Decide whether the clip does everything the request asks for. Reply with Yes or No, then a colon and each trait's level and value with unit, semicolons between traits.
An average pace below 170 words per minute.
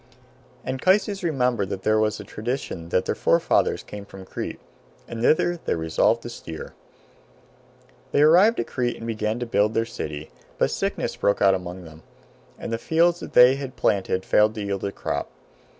No: average, 180 wpm